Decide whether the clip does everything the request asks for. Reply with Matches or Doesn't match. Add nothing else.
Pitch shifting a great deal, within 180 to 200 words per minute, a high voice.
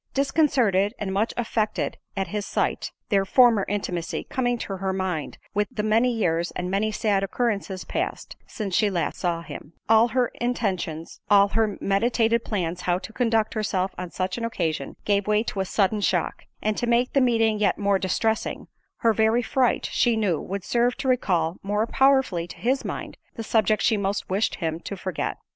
Doesn't match